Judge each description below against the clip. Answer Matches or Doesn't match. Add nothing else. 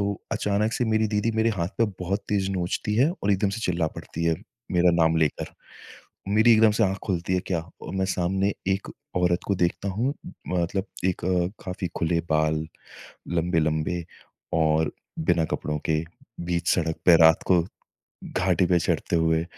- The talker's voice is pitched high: Doesn't match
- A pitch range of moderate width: Matches